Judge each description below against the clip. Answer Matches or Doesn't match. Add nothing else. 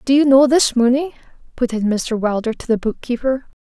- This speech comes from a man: Doesn't match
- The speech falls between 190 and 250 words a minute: Matches